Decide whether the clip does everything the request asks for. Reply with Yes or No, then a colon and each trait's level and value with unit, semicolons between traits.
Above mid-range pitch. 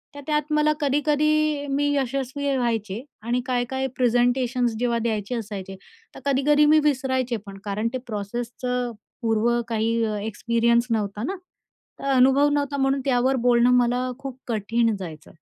Yes: high, 245 Hz